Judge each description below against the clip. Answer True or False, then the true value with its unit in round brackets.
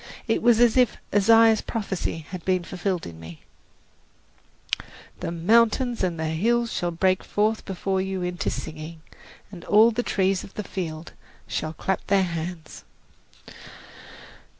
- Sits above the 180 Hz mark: True (190 Hz)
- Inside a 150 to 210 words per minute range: False (140 wpm)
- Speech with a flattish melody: False (4.6 semitones)